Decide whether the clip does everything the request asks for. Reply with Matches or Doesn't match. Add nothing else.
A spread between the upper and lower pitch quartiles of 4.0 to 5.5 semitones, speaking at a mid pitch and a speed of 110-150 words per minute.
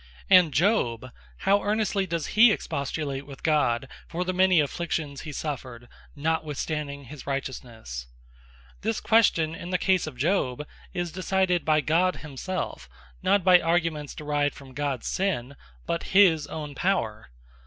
Matches